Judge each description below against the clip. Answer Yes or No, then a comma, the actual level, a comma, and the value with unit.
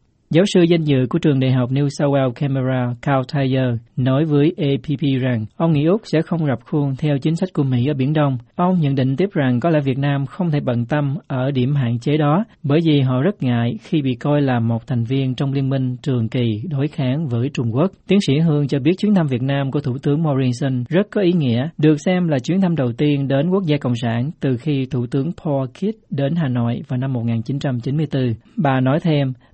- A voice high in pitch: No, medium, 140 Hz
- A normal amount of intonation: Yes, average, 3.3 semitones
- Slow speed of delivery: No, average, 240 wpm